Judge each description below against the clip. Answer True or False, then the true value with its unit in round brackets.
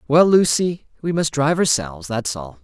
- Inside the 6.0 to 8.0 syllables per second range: False (5.2 syllables/s)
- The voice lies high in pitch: False (135 Hz)